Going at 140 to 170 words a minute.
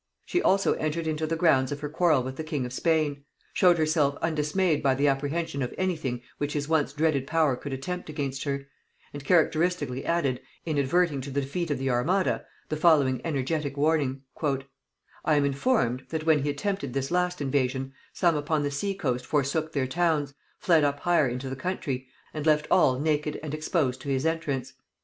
No: average, 190 wpm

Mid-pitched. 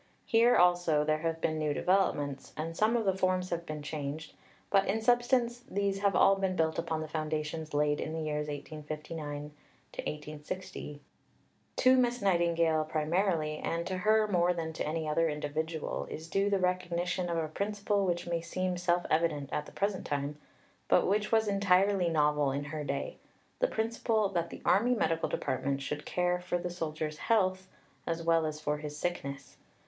Yes: medium, 170 Hz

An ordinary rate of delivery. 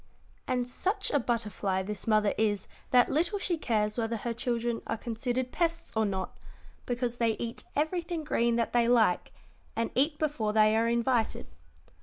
Yes: average, 165 wpm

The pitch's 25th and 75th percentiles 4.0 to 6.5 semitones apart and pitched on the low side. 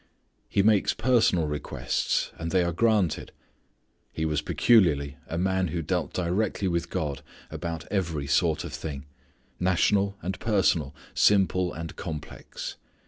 No: average, 3.5 semitones; very low, 90 Hz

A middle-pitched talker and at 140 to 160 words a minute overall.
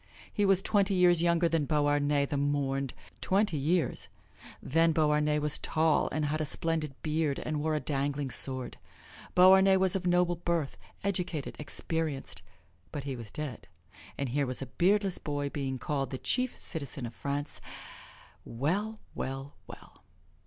Yes: medium, 150 Hz; average, 150 wpm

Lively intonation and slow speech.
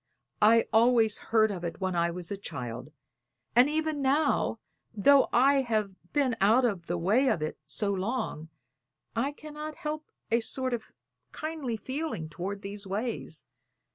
No: wide, 5.9 semitones; average, 155 wpm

